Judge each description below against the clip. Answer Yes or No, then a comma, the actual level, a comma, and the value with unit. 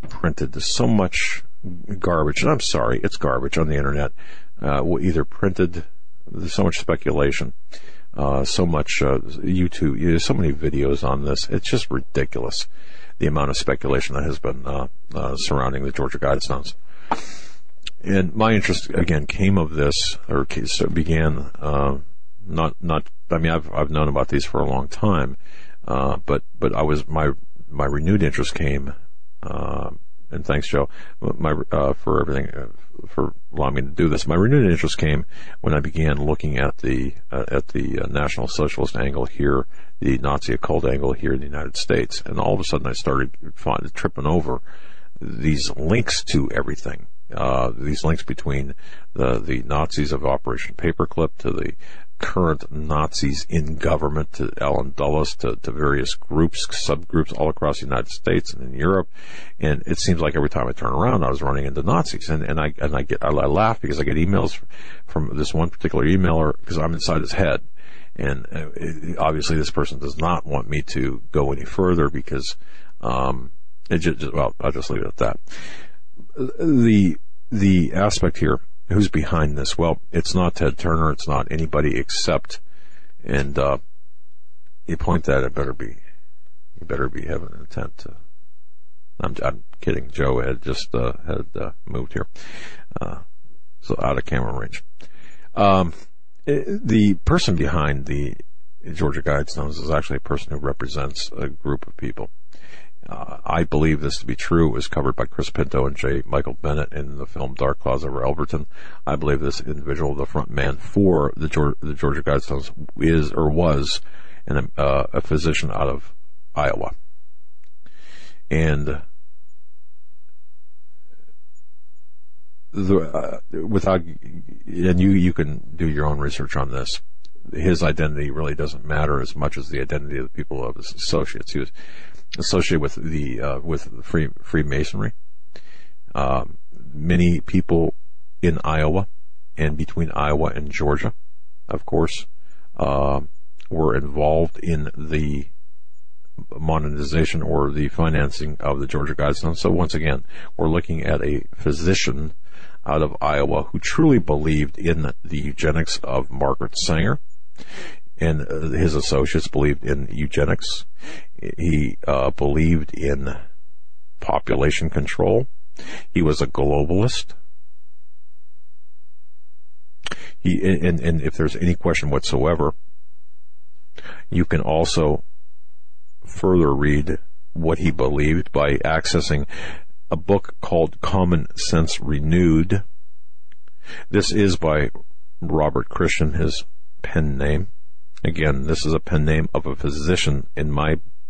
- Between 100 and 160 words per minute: Yes, average, 150 wpm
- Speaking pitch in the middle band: No, very low, 75 Hz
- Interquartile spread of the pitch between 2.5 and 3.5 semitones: Yes, average, 3.0 semitones